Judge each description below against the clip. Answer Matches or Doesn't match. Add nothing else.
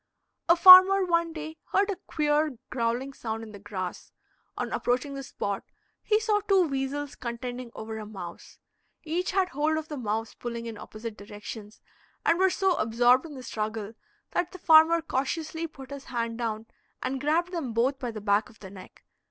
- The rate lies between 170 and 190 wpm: Matches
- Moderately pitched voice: Doesn't match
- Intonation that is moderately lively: Doesn't match